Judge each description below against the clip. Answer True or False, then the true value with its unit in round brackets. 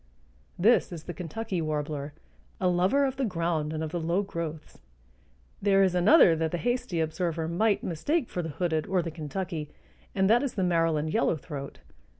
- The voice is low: False (175 Hz)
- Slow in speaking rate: False (175 wpm)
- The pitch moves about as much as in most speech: True (3.6 semitones)